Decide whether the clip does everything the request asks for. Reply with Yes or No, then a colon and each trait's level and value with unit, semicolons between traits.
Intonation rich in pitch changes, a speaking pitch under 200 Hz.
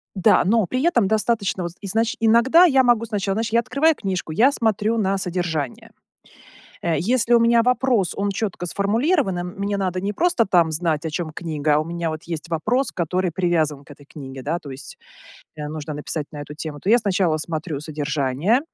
Yes: wide, 6.3 semitones; medium, 185 Hz